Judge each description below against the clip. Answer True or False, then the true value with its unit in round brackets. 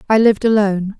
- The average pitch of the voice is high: True (210 Hz)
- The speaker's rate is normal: True (180 wpm)